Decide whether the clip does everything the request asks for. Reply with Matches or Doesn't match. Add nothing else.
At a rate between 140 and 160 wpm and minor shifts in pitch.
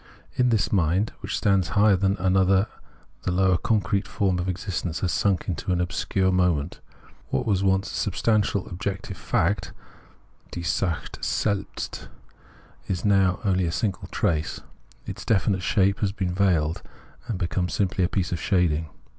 Matches